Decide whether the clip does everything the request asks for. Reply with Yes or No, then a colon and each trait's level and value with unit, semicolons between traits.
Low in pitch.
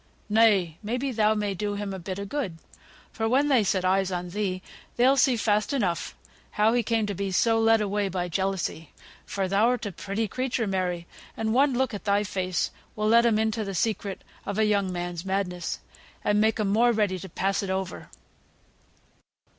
No: high, 205 Hz